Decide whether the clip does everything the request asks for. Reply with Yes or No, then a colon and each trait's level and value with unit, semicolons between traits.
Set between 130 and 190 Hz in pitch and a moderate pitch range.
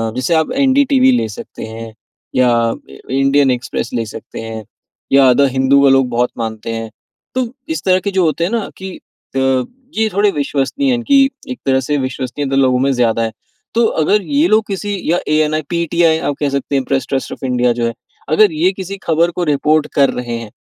No: medium, 140 Hz; wide, 6.7 semitones